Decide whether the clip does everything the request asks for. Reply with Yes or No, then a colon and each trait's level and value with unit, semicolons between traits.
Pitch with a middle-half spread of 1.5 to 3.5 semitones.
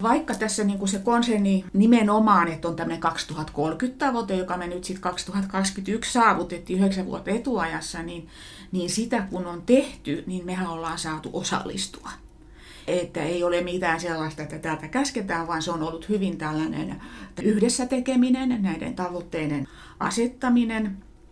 No: average, 4.9 semitones